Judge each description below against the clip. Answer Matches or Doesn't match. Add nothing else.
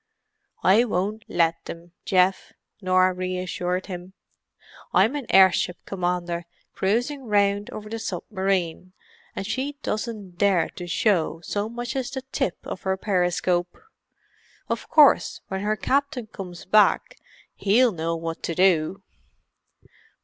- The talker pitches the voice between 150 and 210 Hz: Matches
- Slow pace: Matches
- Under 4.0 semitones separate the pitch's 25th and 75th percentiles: Matches